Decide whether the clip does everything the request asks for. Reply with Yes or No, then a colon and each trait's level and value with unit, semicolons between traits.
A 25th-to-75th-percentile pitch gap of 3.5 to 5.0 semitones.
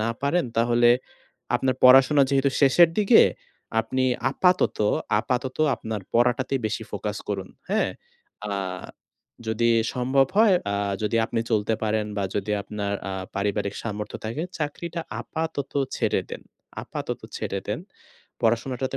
Yes: average, 4.1 semitones